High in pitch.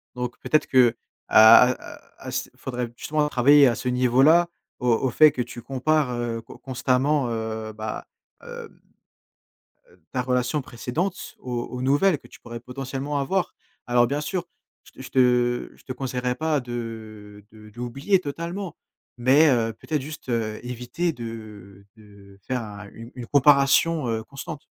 No: low, 125 Hz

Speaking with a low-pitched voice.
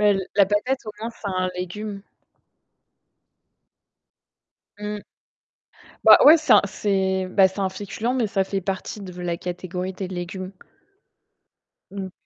No: high, 195 Hz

